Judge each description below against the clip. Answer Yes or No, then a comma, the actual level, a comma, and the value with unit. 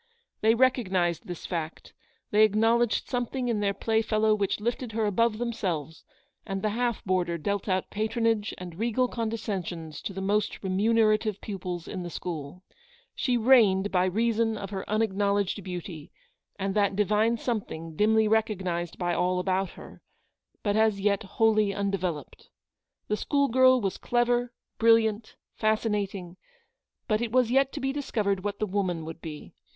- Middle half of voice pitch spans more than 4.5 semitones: No, average, 3.4 semitones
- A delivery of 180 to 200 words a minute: No, average, 155 wpm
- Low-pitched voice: No, high, 210 Hz